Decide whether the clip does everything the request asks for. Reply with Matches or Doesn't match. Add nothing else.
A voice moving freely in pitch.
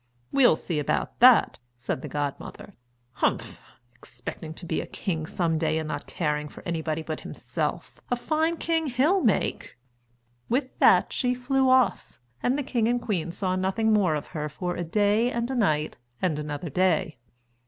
Matches